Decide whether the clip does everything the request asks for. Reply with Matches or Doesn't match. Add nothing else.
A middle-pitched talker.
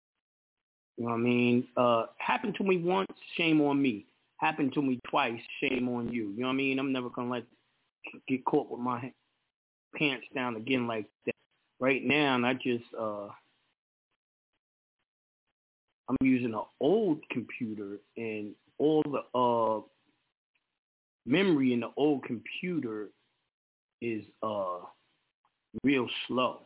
Doesn't match